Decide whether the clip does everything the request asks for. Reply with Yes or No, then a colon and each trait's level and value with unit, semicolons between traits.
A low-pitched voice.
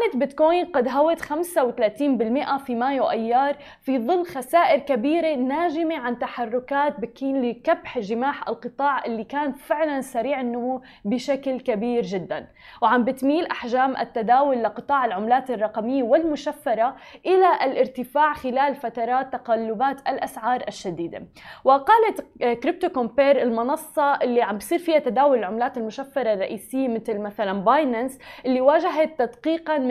No: very high, 265 Hz